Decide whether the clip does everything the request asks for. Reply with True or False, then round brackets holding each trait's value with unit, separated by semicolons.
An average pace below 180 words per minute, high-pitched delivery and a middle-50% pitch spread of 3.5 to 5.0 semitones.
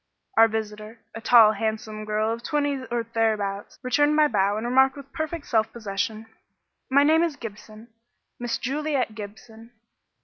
True (150 wpm; 230 Hz; 4.0 semitones)